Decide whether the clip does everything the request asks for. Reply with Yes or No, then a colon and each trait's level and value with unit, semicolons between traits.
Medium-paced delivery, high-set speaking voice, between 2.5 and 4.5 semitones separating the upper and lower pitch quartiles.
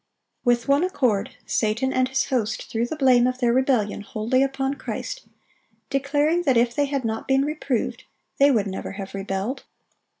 Yes: average, 170 wpm; very high, 255 Hz; average, 3.7 semitones